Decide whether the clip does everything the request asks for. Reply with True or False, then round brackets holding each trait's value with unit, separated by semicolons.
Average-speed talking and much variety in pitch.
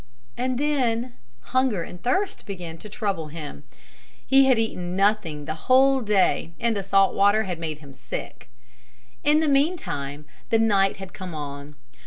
True (160 wpm; 7.4 semitones)